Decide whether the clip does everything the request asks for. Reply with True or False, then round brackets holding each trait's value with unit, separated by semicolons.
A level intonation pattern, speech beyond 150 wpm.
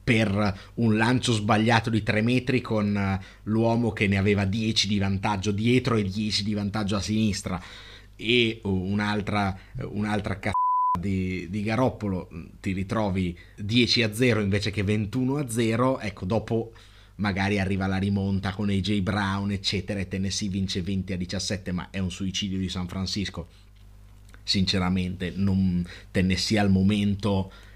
False (2.1 semitones; 145 wpm)